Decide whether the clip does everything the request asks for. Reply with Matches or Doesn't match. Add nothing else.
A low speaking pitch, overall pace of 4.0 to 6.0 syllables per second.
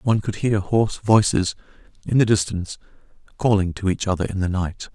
Matches